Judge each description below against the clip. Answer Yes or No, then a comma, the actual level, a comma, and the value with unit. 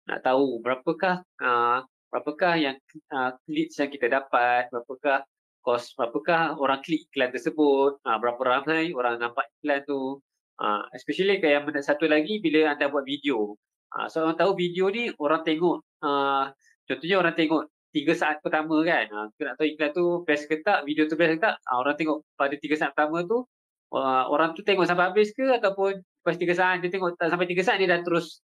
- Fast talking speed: Yes, fast, 205 wpm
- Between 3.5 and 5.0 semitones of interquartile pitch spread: Yes, average, 4.0 semitones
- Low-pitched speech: No, medium, 150 Hz